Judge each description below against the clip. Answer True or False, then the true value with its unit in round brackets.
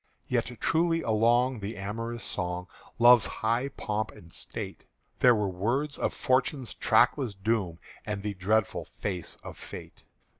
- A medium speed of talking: True (145 wpm)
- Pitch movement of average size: True (3.7 semitones)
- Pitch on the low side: True (110 Hz)